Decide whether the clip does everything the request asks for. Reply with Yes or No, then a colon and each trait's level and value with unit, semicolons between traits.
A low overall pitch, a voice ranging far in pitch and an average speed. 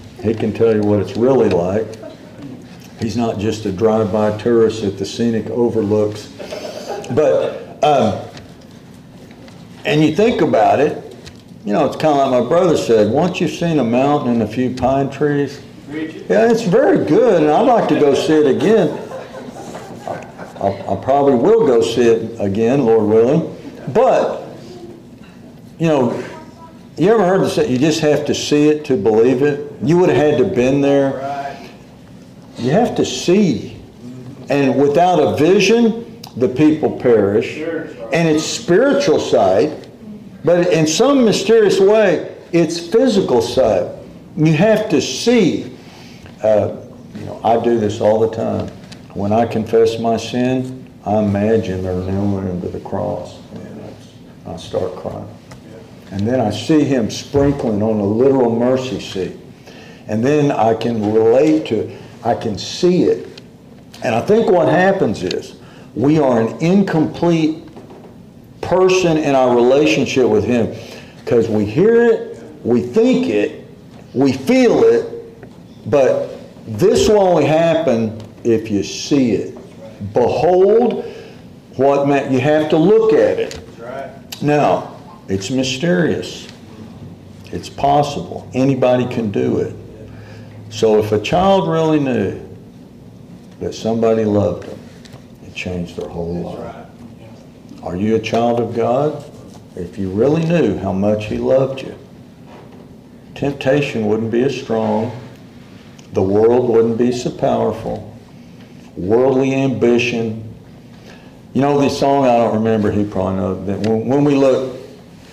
Yes: low, 125 Hz; wide, 5.9 semitones; average, 145 wpm